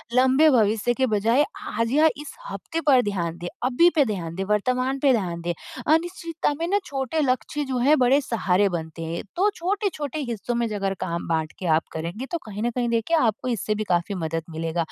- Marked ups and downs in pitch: Yes, wide, 7.0 semitones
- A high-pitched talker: Yes, high, 235 Hz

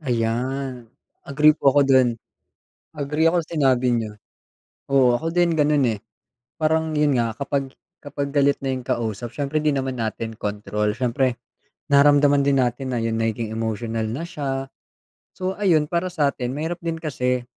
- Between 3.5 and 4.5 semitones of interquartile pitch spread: Yes, average, 3.9 semitones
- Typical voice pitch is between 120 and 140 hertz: Yes, low, 135 Hz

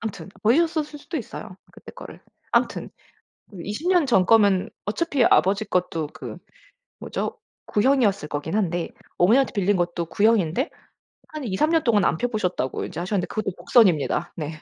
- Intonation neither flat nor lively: No, wide, 6.2 semitones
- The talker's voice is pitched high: Yes, high, 205 Hz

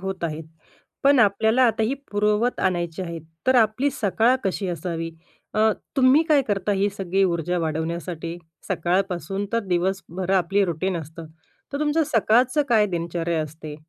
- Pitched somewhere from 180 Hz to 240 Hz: Yes, high, 190 Hz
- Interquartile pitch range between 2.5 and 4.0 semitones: No, average, 4.4 semitones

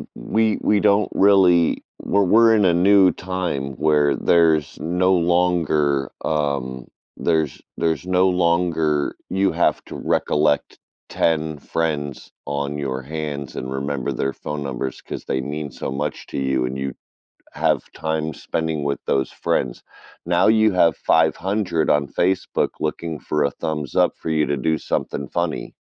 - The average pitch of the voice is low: Yes, very low, 80 Hz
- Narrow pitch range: No, average, 4.0 semitones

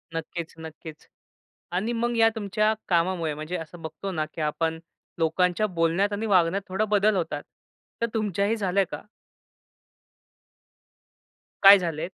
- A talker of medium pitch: Yes, medium, 180 Hz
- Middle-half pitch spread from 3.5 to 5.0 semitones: Yes, average, 3.9 semitones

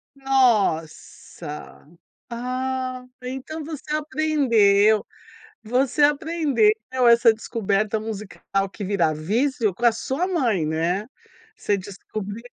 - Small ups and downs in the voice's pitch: No, average, 5.0 semitones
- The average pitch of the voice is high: Yes, high, 230 Hz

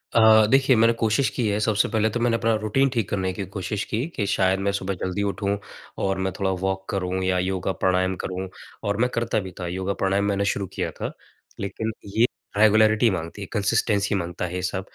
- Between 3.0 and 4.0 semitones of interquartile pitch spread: No, narrow, 2.6 semitones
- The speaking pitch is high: No, low, 100 Hz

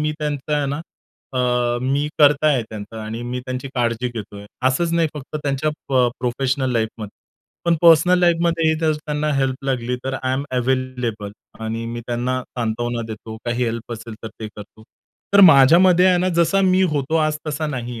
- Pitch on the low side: Yes, low, 130 Hz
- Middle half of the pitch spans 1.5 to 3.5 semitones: No, average, 4.4 semitones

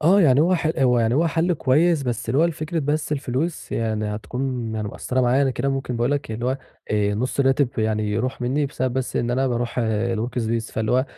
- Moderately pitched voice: No, low, 130 Hz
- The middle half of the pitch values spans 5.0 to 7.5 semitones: No, average, 3.7 semitones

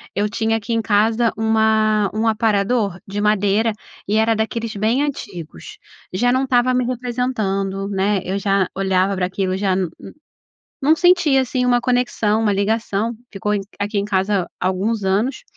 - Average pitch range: Yes, average, 3.0 semitones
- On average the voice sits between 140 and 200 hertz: No, high, 215 Hz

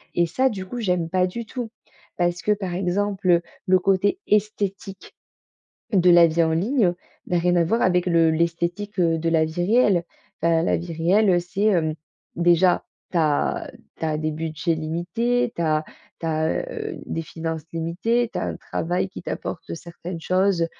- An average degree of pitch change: Yes, average, 3.2 semitones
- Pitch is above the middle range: No, medium, 175 Hz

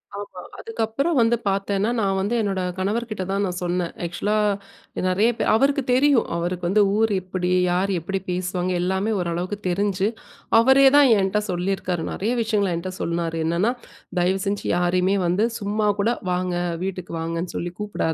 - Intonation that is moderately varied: Yes, average, 3.0 semitones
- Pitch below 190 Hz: No, high, 195 Hz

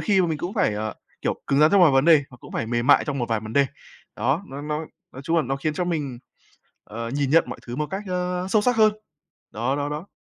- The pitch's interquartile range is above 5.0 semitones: Yes, wide, 5.4 semitones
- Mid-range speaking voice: Yes, medium, 145 Hz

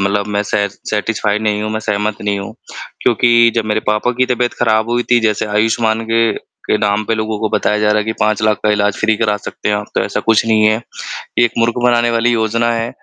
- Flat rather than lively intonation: Yes, narrow, 1.5 semitones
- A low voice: Yes, low, 110 Hz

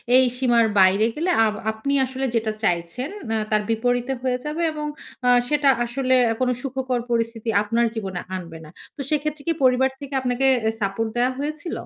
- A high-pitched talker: Yes, very high, 250 Hz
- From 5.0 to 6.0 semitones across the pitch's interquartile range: No, average, 3.5 semitones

